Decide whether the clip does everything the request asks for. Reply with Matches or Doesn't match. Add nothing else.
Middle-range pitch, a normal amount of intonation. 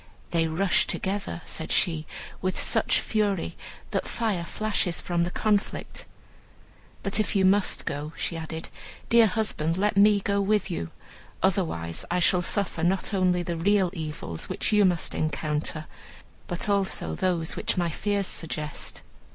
Matches